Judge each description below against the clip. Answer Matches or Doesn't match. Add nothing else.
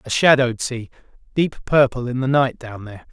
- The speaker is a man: Matches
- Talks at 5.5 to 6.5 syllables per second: Matches